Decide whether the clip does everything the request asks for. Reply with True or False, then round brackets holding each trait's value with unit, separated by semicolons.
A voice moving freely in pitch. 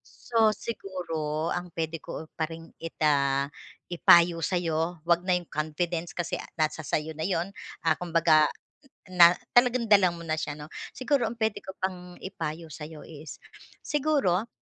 False (2.8 semitones)